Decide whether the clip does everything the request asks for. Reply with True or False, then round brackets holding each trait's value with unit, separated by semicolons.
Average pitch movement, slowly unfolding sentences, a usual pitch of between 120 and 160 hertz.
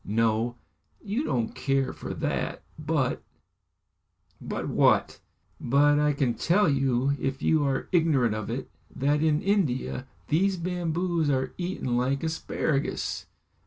True (4.2 semitones; 130 wpm; 140 Hz)